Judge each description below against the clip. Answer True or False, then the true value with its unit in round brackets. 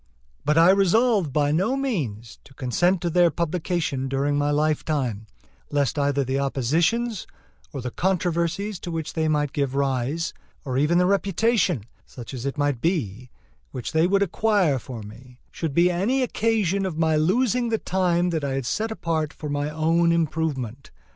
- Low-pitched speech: False (160 Hz)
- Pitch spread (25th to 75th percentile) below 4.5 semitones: False (4.8 semitones)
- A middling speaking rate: True (170 wpm)